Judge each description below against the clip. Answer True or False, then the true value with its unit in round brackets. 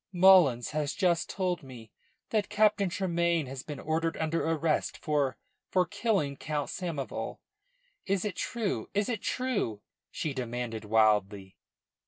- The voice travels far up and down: True (6.3 semitones)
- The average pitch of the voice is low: False (160 Hz)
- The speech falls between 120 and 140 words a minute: True (135 wpm)